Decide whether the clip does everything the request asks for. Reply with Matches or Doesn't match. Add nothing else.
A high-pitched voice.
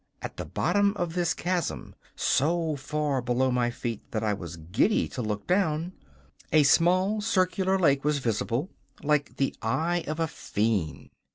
Doesn't match